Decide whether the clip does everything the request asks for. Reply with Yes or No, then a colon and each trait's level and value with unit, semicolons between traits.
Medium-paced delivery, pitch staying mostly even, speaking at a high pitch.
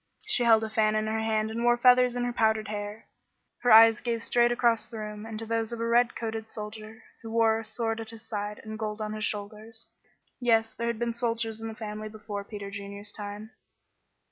No: fast, 220 wpm; narrow, 1.3 semitones; high, 220 Hz